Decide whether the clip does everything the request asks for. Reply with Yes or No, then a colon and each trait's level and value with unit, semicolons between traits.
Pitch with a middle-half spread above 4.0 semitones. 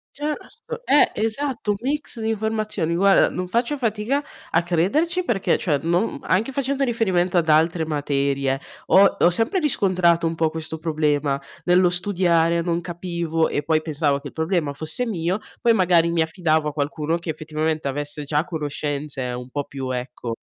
Yes: wide, 5.4 semitones